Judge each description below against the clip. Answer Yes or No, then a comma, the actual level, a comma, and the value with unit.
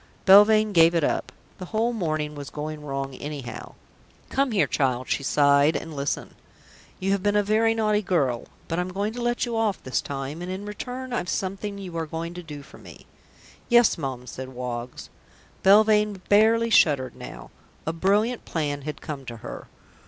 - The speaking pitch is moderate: Yes, medium, 175 Hz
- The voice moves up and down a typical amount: No, wide, 6.7 semitones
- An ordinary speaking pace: Yes, average, 185 wpm